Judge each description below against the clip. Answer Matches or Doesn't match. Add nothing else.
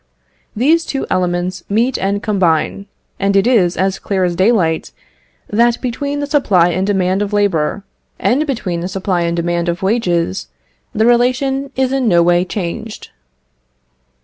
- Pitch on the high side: Matches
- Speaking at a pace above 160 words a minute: Doesn't match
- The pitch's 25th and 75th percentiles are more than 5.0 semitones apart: Matches